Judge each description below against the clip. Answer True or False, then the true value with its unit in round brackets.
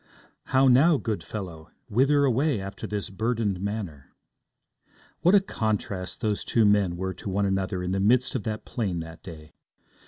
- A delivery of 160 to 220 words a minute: True (165 wpm)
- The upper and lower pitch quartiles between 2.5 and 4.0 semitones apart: False (4.5 semitones)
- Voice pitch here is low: True (105 Hz)